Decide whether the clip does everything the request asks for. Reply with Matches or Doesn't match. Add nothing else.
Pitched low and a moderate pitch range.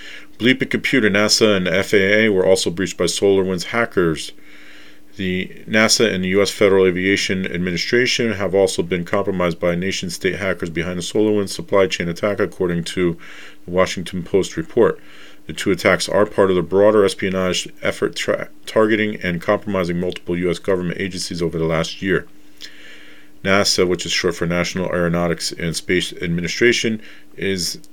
Matches